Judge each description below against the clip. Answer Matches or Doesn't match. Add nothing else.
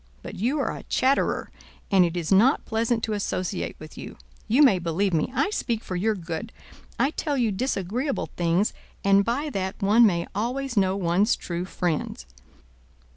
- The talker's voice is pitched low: Doesn't match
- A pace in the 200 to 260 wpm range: Doesn't match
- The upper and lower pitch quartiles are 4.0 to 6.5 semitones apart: Matches